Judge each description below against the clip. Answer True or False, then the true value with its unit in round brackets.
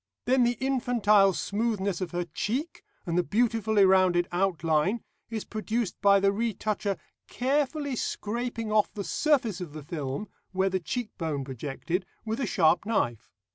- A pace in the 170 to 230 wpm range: False (145 wpm)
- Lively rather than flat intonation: False (4.8 semitones)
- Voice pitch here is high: True (205 Hz)